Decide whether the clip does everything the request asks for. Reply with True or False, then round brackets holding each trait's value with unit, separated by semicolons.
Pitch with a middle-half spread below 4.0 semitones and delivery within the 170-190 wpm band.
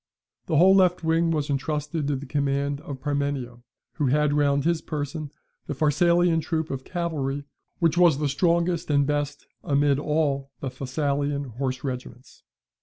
False (2.5 semitones; 155 wpm)